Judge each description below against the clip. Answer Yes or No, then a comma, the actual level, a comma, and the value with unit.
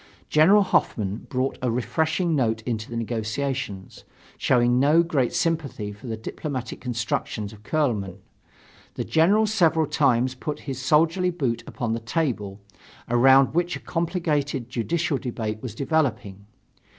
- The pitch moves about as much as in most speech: No, wide, 5.8 semitones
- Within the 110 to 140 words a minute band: Yes, slow, 135 wpm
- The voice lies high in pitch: No, low, 130 Hz